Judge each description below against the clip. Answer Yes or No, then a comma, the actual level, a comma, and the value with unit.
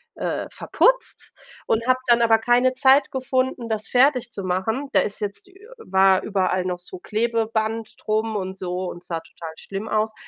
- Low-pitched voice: No, high, 220 Hz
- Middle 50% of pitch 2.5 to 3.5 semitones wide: No, average, 4.5 semitones